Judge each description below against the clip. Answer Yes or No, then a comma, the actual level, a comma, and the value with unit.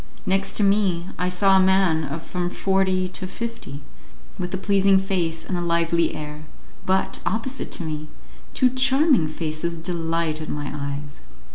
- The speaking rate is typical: Yes, average, 155 wpm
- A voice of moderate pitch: Yes, medium, 180 Hz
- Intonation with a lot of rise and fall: No, average, 3.2 semitones